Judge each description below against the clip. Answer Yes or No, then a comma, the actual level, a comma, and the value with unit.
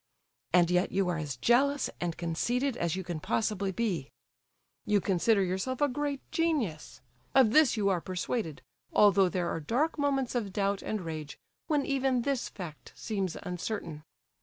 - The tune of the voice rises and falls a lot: Yes, wide, 6.4 semitones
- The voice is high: Yes, high, 200 Hz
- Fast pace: No, average, 160 wpm